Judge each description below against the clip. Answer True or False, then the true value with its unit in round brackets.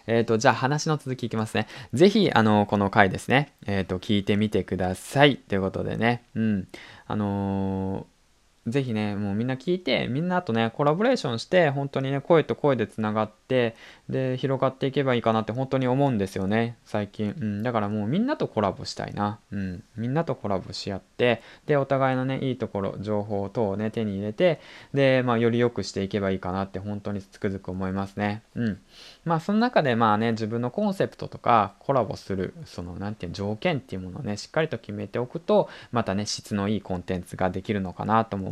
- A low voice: True (110 Hz)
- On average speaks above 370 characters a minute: True (420 characters per minute)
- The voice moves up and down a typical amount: True (4.7 semitones)